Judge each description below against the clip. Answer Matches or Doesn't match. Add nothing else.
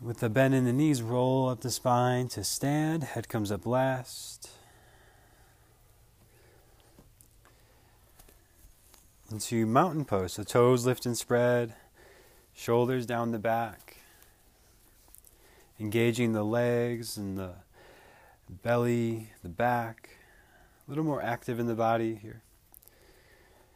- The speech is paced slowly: Matches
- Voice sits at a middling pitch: Doesn't match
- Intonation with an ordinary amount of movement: Doesn't match